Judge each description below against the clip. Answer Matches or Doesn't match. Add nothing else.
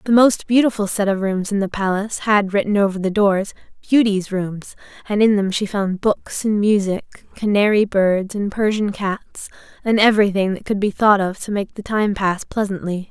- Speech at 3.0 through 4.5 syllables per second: Doesn't match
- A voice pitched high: Matches